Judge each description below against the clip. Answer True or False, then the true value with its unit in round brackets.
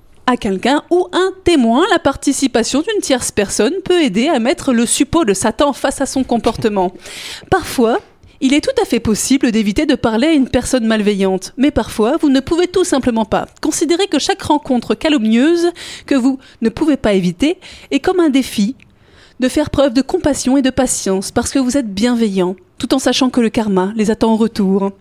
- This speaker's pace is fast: False (195 wpm)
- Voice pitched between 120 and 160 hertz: False (265 Hz)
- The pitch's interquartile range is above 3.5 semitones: True (4.9 semitones)